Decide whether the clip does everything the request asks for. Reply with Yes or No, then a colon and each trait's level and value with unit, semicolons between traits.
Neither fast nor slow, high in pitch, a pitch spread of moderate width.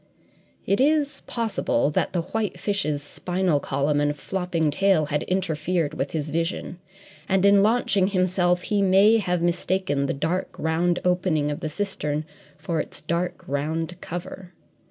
No: average, 150 wpm; medium, 175 Hz; average, 4.0 semitones